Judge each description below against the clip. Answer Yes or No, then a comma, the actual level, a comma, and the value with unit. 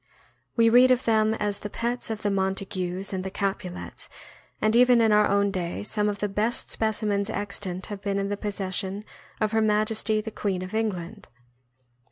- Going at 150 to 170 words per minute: No, average, 190 wpm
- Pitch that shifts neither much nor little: No, narrow, 2.0 semitones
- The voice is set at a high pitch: Yes, high, 205 Hz